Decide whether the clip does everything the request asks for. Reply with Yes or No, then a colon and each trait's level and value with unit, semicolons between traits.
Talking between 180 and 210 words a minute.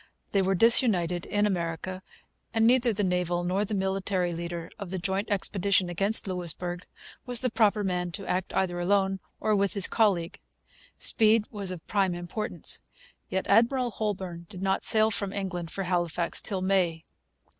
No: average, 165 wpm